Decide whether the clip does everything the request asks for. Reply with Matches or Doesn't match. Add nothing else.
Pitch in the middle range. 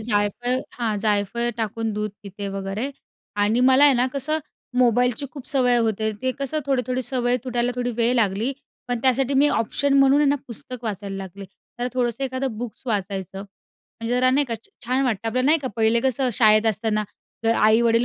Doesn't match